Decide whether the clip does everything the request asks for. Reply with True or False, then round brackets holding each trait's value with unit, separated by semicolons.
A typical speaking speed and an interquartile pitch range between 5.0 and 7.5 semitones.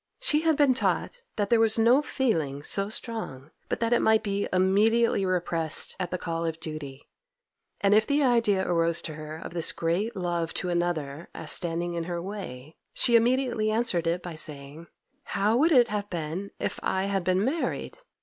True (185 wpm; 5.5 semitones)